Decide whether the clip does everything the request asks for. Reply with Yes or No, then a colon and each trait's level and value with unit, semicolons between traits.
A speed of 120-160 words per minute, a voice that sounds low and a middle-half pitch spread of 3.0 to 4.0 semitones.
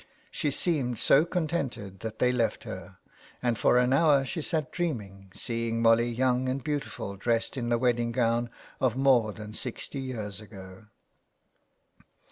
Yes: average, 150 wpm; low, 120 Hz; average, 3.4 semitones